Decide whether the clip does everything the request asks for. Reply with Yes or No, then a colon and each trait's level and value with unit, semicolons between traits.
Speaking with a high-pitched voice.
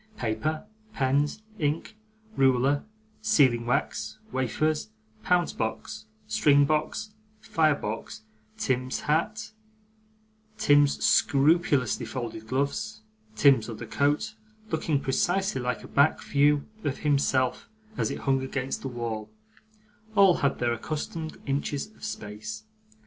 No: medium, 140 Hz